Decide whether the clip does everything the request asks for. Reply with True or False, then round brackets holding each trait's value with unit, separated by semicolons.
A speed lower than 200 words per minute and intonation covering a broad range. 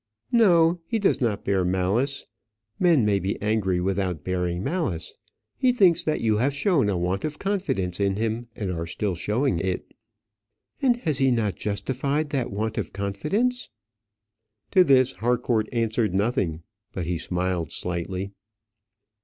True (150 wpm; 7.2 semitones)